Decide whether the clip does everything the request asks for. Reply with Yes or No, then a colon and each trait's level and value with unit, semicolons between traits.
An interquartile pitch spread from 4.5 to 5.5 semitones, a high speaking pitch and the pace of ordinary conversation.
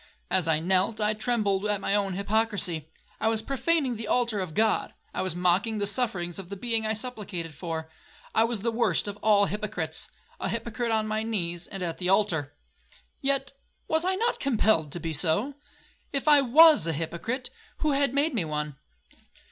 Yes: average, 4.9 semitones; high, 210 Hz; average, 180 wpm